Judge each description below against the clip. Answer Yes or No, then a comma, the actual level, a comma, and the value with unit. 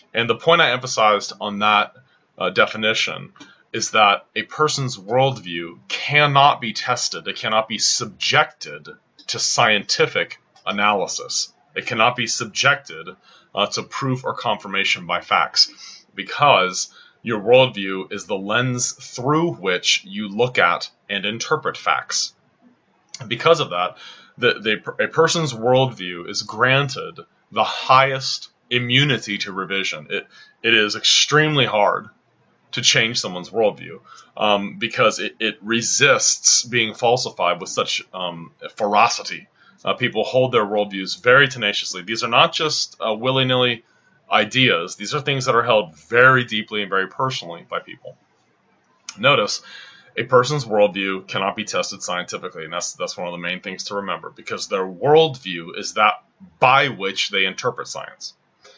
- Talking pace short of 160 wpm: Yes, average, 145 wpm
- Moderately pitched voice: No, low, 125 Hz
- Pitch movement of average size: No, wide, 5.7 semitones